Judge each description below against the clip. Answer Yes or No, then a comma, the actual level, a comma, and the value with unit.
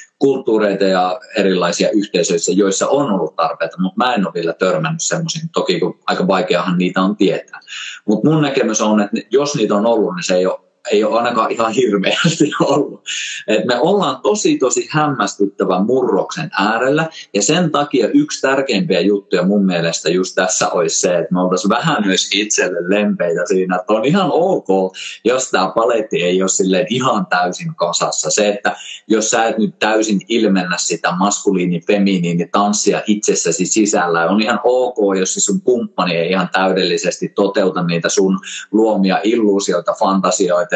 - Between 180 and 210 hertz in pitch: No, low, 100 Hz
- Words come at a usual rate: No, fast, 160 wpm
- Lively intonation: Yes, wide, 6.6 semitones